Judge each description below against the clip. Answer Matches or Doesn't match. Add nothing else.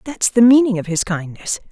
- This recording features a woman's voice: Matches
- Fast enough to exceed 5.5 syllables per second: Doesn't match